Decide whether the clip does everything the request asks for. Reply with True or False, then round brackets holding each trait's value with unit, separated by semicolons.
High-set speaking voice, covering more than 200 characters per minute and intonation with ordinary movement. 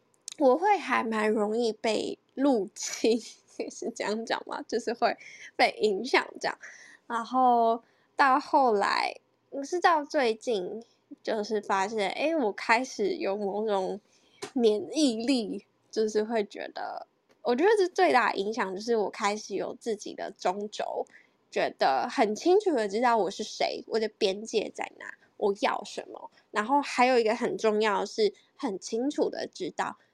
True (230 Hz; 215 characters per minute; 4.9 semitones)